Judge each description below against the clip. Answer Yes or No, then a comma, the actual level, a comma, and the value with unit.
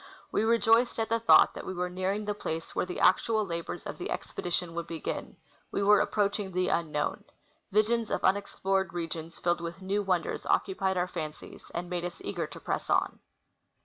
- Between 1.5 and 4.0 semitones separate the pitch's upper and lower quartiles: Yes, average, 3.3 semitones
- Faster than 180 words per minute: Yes, average, 190 wpm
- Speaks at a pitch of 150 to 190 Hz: Yes, medium, 185 Hz